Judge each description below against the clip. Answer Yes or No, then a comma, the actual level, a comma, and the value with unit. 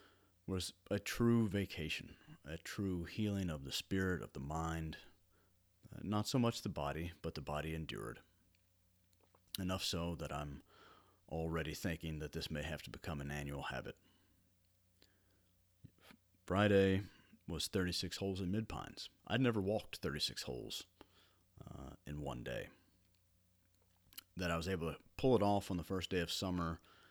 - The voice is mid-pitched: No, very low, 90 Hz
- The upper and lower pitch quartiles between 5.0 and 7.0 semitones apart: No, average, 2.8 semitones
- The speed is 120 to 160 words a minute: Yes, average, 150 wpm